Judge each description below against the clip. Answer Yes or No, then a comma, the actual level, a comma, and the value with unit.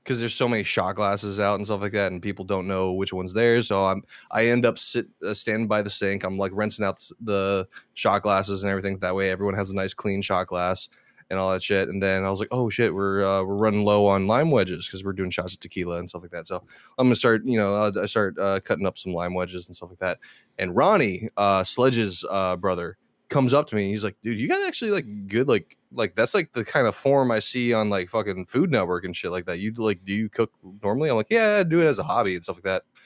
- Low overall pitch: Yes, low, 100 Hz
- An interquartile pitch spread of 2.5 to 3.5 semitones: Yes, average, 2.8 semitones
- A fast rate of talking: Yes, fast, 275 wpm